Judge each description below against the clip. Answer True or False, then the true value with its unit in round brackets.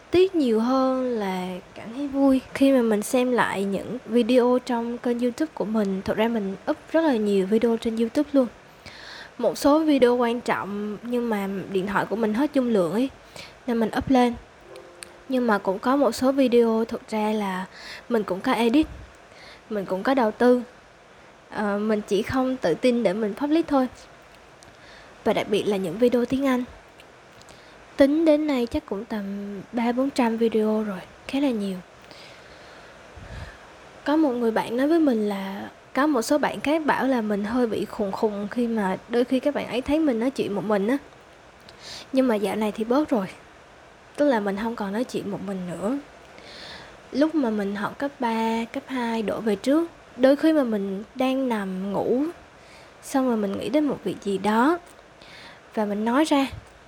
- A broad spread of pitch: False (4.3 semitones)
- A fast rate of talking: False (190 wpm)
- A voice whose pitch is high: True (235 Hz)